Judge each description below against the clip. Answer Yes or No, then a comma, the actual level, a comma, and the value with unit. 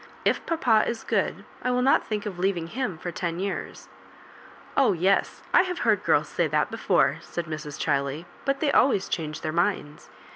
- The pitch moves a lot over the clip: Yes, wide, 7.3 semitones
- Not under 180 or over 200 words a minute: Yes, average, 185 wpm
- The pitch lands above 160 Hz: Yes, high, 190 Hz